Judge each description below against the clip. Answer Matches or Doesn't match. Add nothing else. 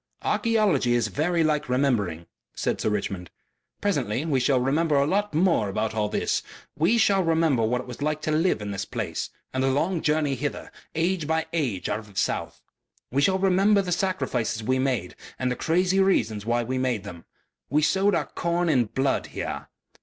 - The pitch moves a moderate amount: Doesn't match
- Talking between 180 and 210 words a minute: Matches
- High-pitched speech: Doesn't match